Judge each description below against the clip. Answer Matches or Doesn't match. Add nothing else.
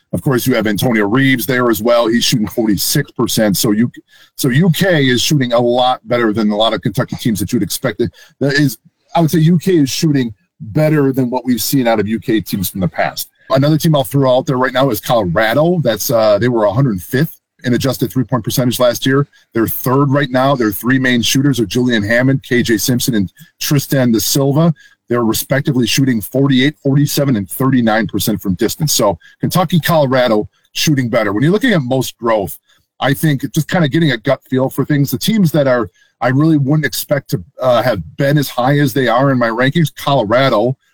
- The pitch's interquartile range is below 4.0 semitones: Matches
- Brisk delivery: Matches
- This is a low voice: Matches